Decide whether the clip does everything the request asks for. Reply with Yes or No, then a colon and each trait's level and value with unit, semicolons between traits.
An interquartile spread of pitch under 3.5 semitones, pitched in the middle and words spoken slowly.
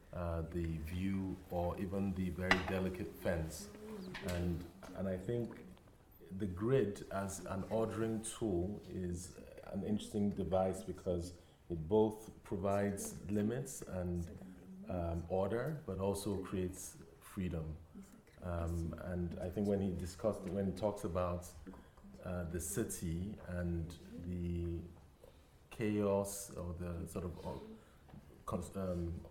No: narrow, 2.4 semitones; very low, 95 Hz; slow, 115 wpm